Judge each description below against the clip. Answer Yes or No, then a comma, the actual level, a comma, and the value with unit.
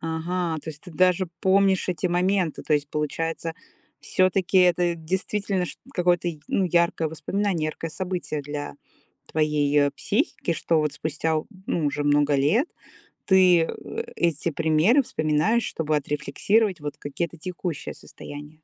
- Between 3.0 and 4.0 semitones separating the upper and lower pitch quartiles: Yes, average, 3.3 semitones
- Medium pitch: Yes, medium, 165 Hz